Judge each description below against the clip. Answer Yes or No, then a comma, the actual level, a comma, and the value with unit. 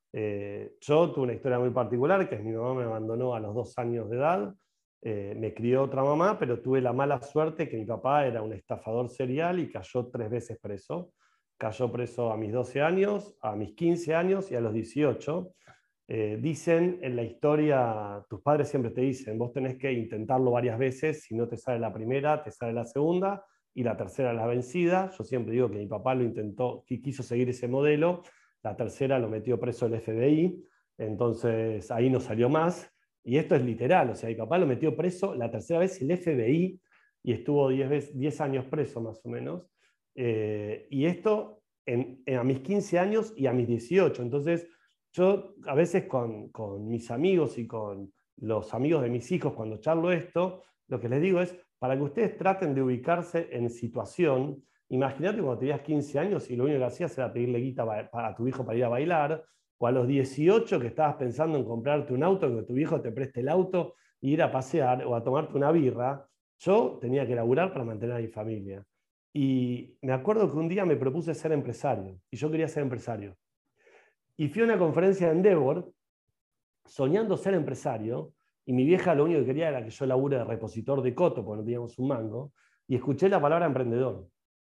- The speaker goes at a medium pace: No, fast, 205 wpm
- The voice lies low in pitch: Yes, low, 130 Hz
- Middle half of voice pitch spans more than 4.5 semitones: Yes, average, 5.0 semitones